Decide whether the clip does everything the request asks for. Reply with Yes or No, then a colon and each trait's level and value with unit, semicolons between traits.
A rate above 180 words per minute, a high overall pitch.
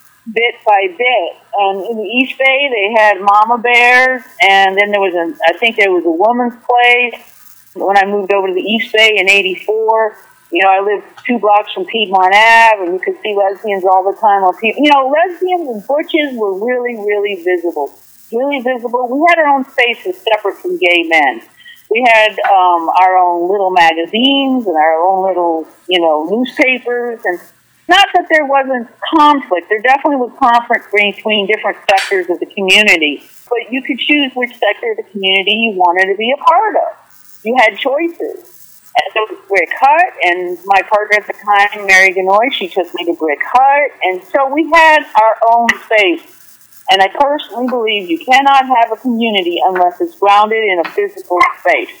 Yes: average, 190 wpm; high, 220 Hz